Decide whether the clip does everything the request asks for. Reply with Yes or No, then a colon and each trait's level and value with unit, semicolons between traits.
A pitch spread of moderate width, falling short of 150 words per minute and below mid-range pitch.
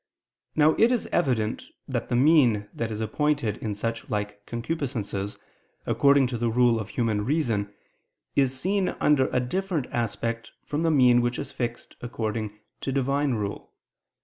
No: average, 4.3 semitones; average, 155 wpm; low, 120 Hz